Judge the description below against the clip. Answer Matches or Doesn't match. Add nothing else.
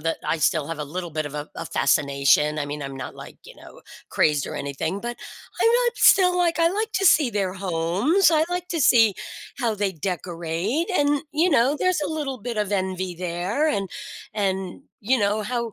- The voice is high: Matches